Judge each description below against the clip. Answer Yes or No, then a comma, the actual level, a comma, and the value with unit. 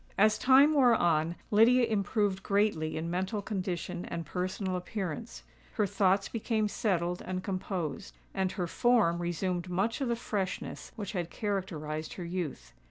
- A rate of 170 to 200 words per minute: No, average, 150 wpm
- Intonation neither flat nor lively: Yes, average, 3.5 semitones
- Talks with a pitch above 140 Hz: Yes, high, 190 Hz